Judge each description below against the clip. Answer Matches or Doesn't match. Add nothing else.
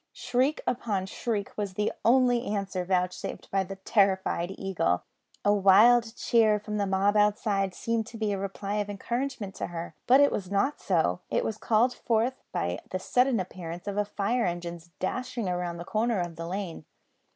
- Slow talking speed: Doesn't match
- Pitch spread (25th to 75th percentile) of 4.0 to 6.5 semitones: Doesn't match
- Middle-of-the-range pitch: Doesn't match